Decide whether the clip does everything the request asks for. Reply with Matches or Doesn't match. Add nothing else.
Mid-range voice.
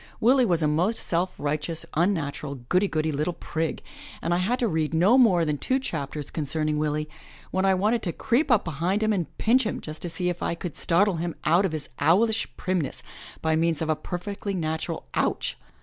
Matches